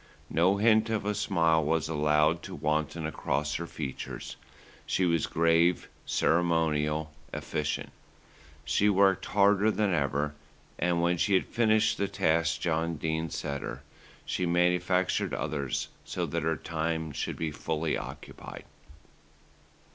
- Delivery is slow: Yes, slow, 130 wpm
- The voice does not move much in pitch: No, average, 3.0 semitones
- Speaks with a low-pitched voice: Yes, very low, 80 Hz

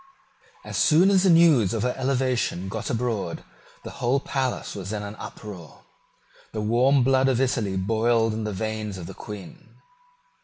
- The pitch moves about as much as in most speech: Yes, average, 4.0 semitones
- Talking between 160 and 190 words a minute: Yes, average, 165 wpm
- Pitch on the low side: Yes, low, 115 Hz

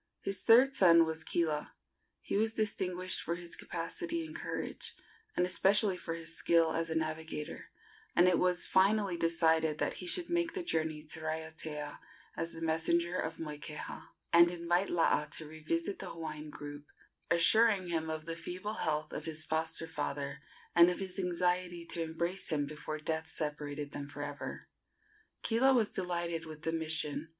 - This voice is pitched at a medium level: Yes, medium, 165 Hz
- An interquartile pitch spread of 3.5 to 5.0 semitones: No, narrow, 2.4 semitones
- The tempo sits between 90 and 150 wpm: No, average, 165 wpm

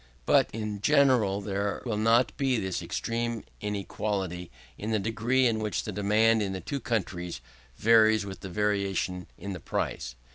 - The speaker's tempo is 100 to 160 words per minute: Yes, average, 155 wpm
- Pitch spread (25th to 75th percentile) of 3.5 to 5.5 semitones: No, narrow, 2.6 semitones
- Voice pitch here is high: No, low, 105 Hz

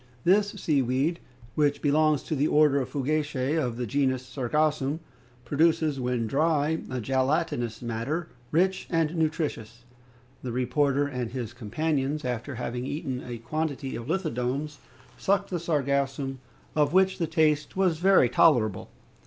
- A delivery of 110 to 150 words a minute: Yes, average, 140 wpm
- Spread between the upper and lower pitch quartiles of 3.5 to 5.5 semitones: Yes, average, 3.8 semitones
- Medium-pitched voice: Yes, medium, 145 Hz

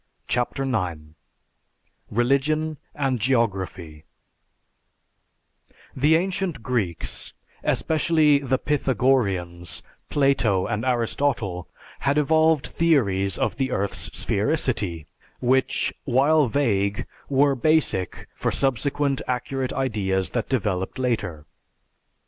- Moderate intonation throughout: No, wide, 6.3 semitones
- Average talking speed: No, slow, 90 wpm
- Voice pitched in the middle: No, low, 125 Hz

